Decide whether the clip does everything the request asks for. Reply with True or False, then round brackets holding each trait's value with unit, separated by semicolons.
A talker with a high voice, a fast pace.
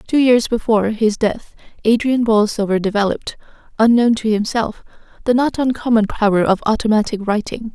False (225 Hz; 140 wpm)